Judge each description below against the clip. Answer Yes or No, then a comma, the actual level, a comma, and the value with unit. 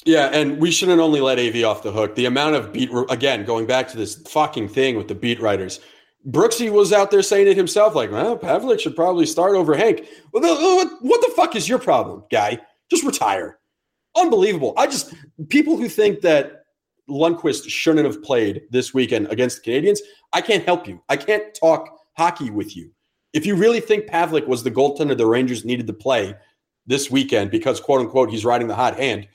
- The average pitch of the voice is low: No, medium, 160 Hz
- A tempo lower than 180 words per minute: No, average, 200 wpm